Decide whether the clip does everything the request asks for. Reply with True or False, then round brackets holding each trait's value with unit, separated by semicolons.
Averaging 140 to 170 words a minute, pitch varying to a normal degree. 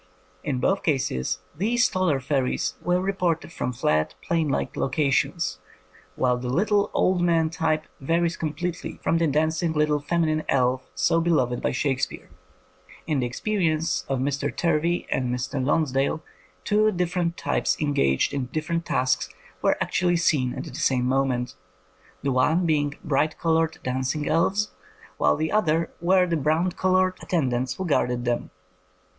True (150 wpm; 4.7 semitones)